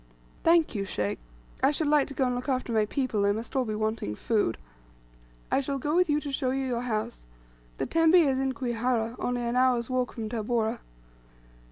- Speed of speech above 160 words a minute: Yes, fast, 205 wpm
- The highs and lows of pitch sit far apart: No, average, 3.5 semitones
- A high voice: Yes, very high, 250 Hz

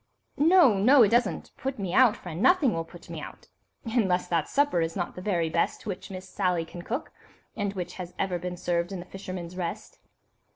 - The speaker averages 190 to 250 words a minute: Yes, fast, 205 wpm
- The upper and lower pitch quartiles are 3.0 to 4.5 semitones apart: Yes, average, 4.0 semitones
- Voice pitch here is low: No, medium, 185 Hz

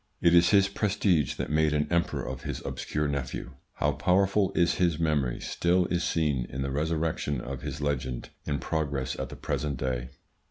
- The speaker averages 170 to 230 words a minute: Yes, average, 185 wpm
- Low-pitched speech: Yes, very low, 75 Hz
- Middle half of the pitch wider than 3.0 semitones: Yes, average, 4.1 semitones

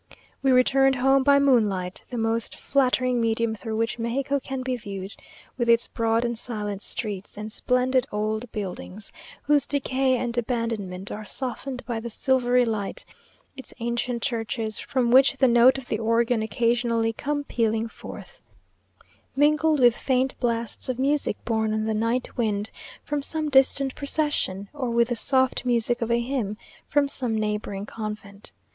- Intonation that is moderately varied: Yes, average, 3.0 semitones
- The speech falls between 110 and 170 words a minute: Yes, average, 160 wpm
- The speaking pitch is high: Yes, high, 235 Hz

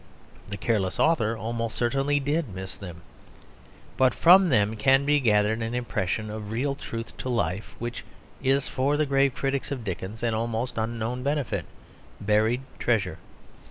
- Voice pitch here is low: Yes, low, 115 Hz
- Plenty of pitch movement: No, average, 4.2 semitones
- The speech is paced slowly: No, average, 155 wpm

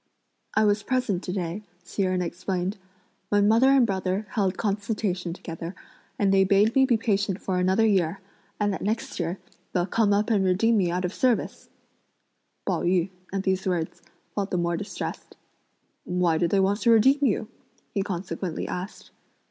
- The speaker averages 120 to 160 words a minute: No, average, 170 wpm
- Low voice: No, high, 195 Hz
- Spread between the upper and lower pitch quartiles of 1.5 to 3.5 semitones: Yes, average, 2.7 semitones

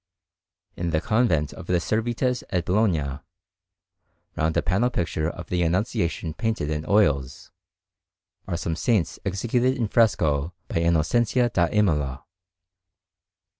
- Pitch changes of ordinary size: No, wide, 5.8 semitones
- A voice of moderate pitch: No, very low, 90 Hz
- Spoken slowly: Yes, slow, 125 wpm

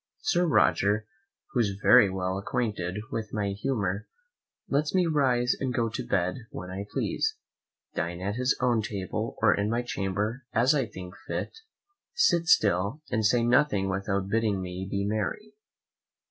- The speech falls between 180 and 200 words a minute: No, average, 160 wpm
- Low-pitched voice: Yes, low, 105 Hz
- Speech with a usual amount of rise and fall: Yes, average, 4.3 semitones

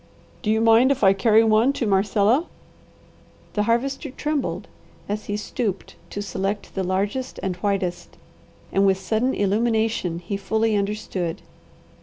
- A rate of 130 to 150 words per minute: Yes, average, 140 wpm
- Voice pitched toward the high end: Yes, high, 210 Hz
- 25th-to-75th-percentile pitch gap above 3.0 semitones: No, average, 2.7 semitones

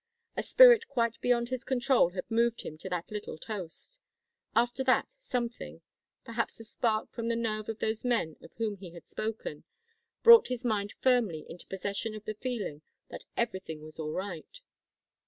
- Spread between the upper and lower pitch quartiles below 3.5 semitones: No, average, 4.1 semitones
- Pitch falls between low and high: No, high, 225 Hz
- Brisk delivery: No, average, 175 wpm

